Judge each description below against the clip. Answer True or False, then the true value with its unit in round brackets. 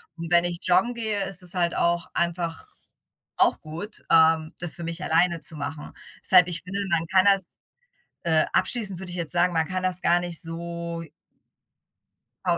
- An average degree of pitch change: False (1.8 semitones)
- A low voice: False (175 Hz)